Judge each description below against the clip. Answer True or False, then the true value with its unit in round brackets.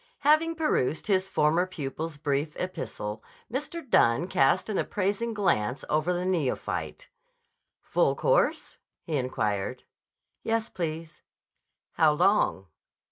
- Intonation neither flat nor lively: False (6.5 semitones)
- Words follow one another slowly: True (110 wpm)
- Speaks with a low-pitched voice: False (170 Hz)